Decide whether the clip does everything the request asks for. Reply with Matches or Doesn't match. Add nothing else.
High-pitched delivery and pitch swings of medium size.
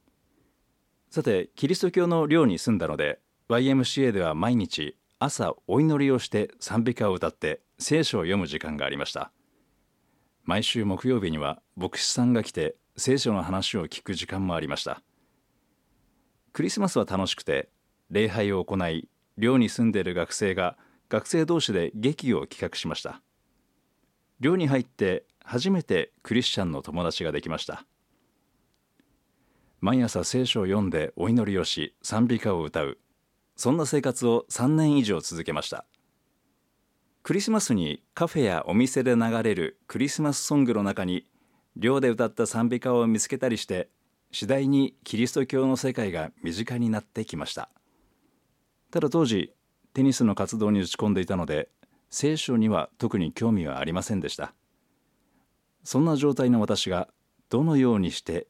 Doesn't match